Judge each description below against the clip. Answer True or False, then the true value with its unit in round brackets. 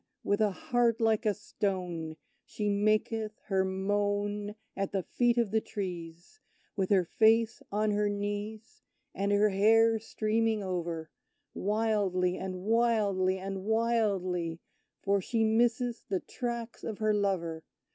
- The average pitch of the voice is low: False (205 Hz)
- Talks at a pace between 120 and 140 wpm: True (135 wpm)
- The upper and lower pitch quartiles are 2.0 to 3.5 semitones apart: True (2.7 semitones)